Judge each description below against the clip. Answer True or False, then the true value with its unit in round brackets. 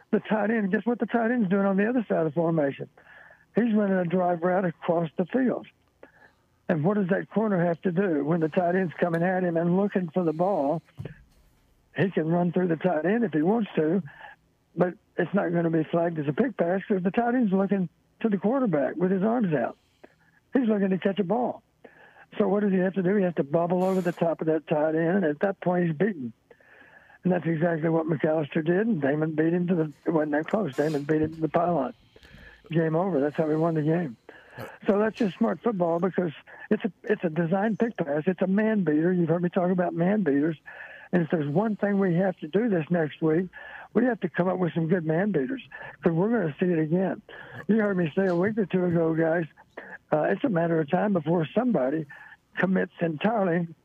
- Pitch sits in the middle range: True (180 Hz)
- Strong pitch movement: False (3.4 semitones)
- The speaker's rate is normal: False (235 wpm)